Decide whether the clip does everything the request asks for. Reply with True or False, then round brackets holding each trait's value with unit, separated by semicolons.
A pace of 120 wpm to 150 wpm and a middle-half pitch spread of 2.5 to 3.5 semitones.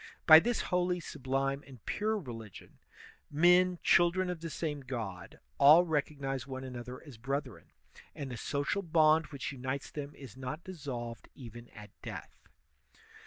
False (145 wpm; 4.5 semitones)